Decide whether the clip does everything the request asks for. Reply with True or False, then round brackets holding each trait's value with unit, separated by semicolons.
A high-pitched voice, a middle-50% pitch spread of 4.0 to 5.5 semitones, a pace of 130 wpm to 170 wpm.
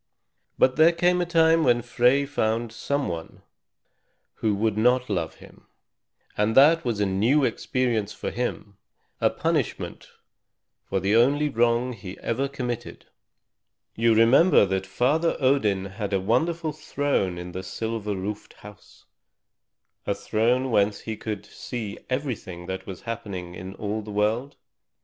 False (115 Hz; 4.7 semitones; 145 wpm)